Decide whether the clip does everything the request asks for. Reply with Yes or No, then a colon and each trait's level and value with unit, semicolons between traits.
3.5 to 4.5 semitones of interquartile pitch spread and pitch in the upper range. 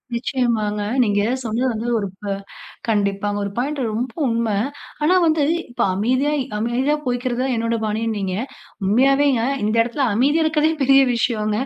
Yes: average, 3.8 semitones; high, 235 Hz